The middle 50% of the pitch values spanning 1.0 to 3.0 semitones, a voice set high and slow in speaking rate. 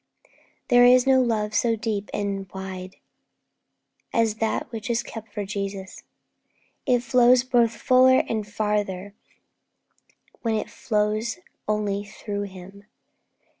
Yes: average, 2.7 semitones; high, 215 Hz; slow, 120 wpm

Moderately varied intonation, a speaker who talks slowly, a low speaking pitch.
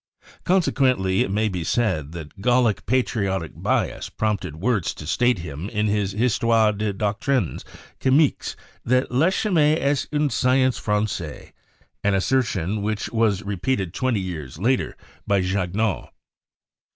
Yes: average, 4.9 semitones; slow, 130 wpm; low, 105 Hz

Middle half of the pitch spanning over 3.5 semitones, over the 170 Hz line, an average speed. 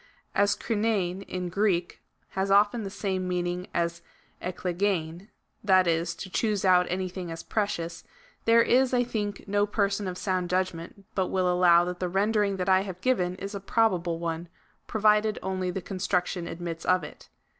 No: narrow, 2.5 semitones; medium, 185 Hz; average, 165 wpm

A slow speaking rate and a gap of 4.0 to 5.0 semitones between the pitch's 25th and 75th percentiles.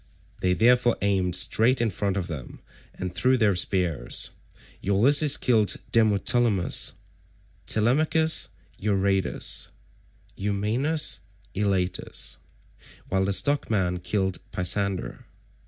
Yes: slow, 90 wpm; average, 4.3 semitones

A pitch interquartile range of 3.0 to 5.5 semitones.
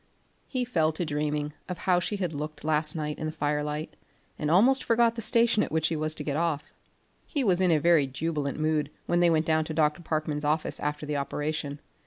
No: narrow, 2.6 semitones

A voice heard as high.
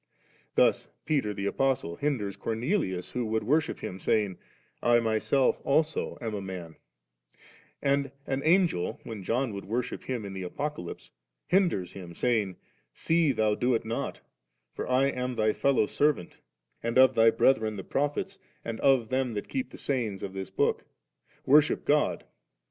No: low, 120 Hz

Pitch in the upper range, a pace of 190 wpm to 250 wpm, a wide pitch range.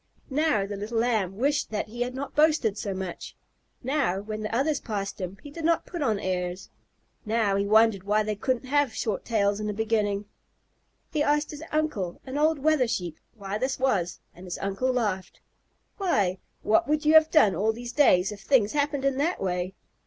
Yes: high, 220 Hz; average, 195 wpm; wide, 6.2 semitones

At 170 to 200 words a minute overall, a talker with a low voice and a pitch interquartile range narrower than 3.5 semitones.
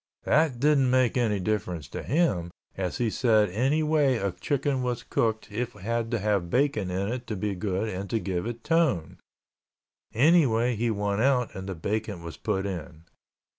No: average, 180 wpm; low, 110 Hz; average, 4.6 semitones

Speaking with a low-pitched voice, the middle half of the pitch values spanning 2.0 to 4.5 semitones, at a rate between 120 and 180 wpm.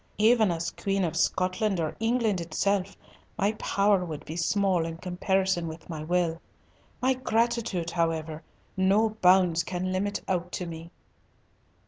No: medium, 185 Hz; average, 3.2 semitones; average, 140 wpm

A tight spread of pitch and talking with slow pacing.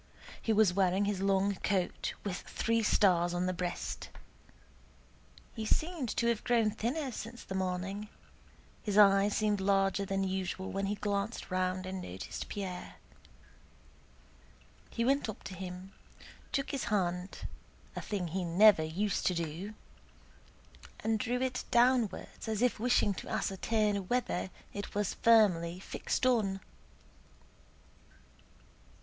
No: average, 3.0 semitones; slow, 130 wpm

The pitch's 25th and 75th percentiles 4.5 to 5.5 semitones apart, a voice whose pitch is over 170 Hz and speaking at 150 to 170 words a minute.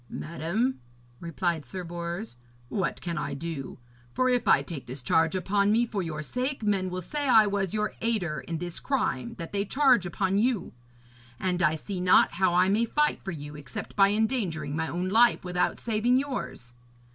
No: average, 4.9 semitones; medium, 185 Hz; average, 185 wpm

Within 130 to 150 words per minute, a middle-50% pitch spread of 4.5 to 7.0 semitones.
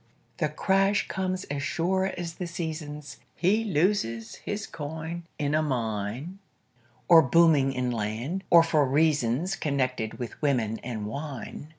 Yes: slow, 135 wpm; average, 5.3 semitones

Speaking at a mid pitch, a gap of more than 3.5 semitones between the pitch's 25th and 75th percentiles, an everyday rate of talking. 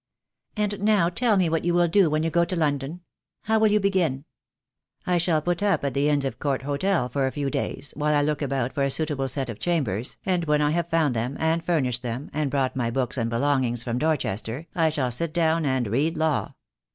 No: medium, 150 Hz; average, 4.3 semitones; fast, 235 wpm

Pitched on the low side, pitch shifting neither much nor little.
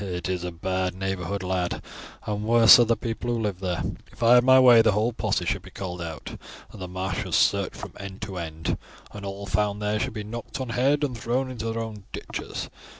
Yes: low, 105 Hz; average, 3.9 semitones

